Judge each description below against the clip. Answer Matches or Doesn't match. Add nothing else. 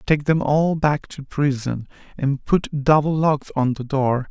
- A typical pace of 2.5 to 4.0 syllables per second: Matches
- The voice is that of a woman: Doesn't match